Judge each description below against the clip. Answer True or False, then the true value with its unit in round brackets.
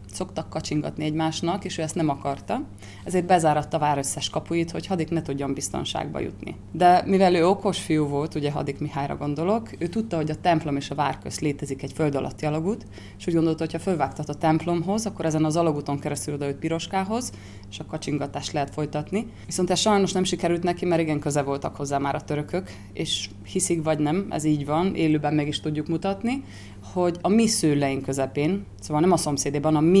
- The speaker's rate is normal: False (200 wpm)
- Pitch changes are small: False (3.5 semitones)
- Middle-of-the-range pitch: True (155 Hz)